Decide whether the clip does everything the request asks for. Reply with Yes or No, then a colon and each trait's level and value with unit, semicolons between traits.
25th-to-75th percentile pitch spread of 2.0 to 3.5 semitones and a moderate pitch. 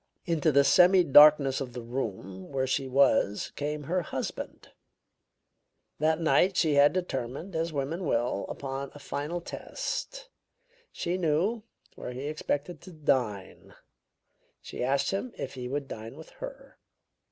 No: average, 4.3 semitones; medium, 145 Hz